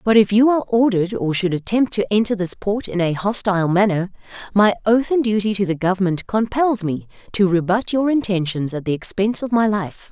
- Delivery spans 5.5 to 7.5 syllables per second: Yes, 5.7 syllables/s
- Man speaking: No, female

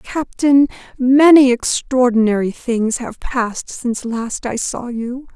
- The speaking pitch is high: Yes, very high, 250 Hz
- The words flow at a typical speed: No, slow, 125 wpm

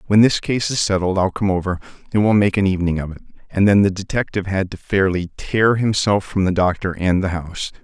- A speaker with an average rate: No, fast, 230 wpm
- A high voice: No, very low, 95 Hz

